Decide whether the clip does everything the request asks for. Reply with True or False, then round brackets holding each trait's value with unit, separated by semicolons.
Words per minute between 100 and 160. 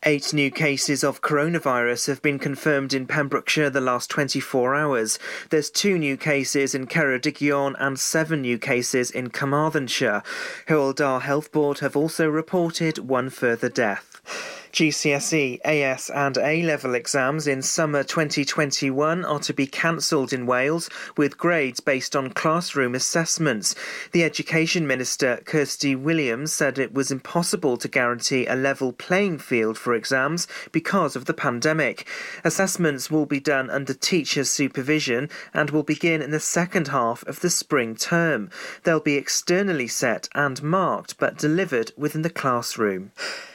True (145 wpm)